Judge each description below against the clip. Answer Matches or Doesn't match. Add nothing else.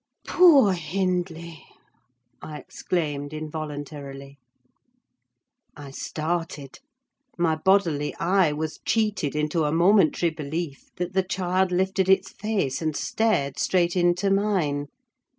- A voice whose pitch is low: Doesn't match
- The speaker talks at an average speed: Doesn't match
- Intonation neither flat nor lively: Matches